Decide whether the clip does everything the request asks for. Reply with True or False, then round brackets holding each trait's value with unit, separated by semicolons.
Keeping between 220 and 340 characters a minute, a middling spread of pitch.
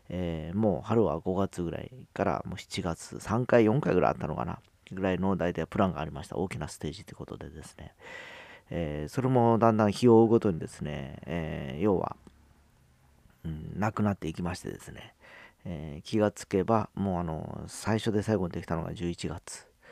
False (360 characters per minute; 4.4 semitones)